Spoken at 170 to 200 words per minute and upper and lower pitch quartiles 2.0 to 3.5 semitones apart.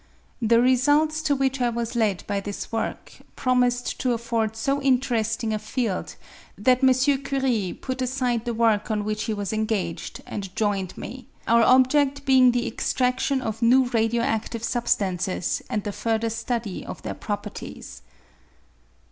No: average, 155 wpm; average, 2.9 semitones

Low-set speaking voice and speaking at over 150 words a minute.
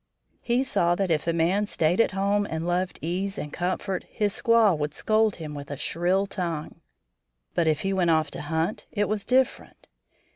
No: medium, 180 Hz; average, 190 wpm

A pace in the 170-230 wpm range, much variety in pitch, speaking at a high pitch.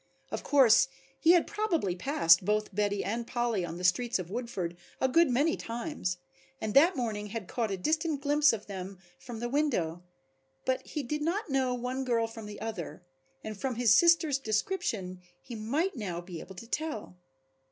Yes: average, 185 wpm; wide, 6.1 semitones; high, 230 Hz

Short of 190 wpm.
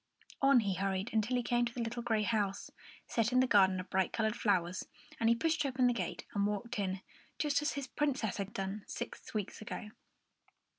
No: fast, 205 wpm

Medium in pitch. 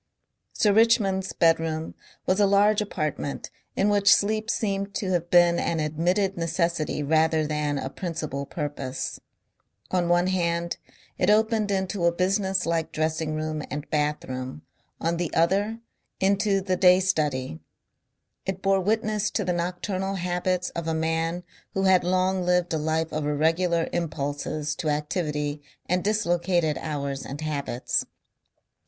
Yes: medium, 175 Hz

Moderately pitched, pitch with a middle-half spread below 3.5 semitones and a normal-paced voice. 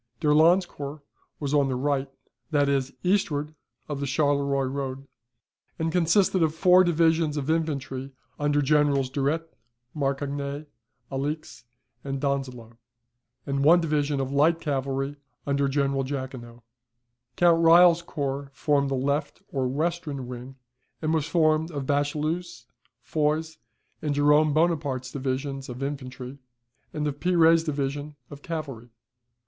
No: medium, 145 Hz; narrow, 2.5 semitones; slow, 130 wpm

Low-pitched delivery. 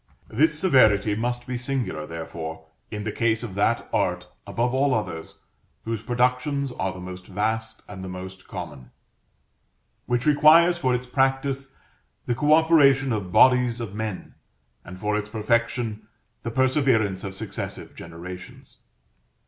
Yes: low, 115 Hz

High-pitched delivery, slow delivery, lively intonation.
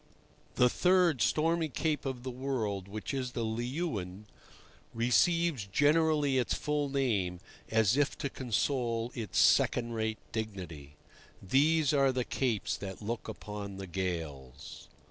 No: low, 120 Hz; slow, 130 wpm; wide, 5.8 semitones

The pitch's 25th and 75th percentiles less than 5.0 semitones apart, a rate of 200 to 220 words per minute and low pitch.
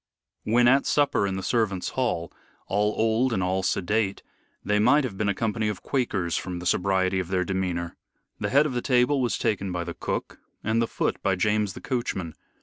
Yes: average, 4.2 semitones; fast, 205 wpm; low, 105 Hz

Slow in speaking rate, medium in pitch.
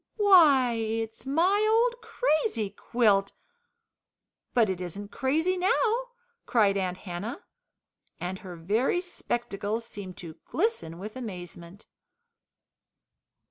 No: slow, 100 wpm; high, 225 Hz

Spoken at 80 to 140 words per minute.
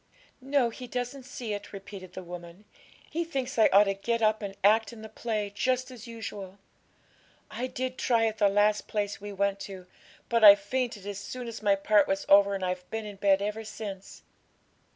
No: average, 200 wpm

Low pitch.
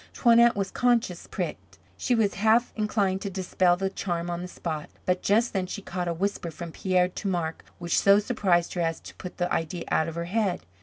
No: medium, 185 Hz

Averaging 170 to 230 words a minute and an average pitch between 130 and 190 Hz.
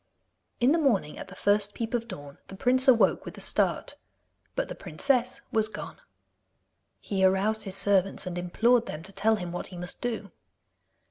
No: average, 185 wpm; high, 205 Hz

